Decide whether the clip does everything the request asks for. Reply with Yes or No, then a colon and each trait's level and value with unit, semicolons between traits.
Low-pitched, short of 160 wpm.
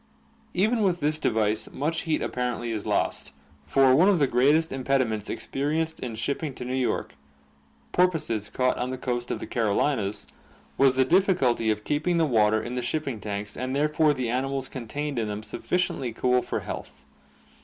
No: low, 130 Hz; average, 175 wpm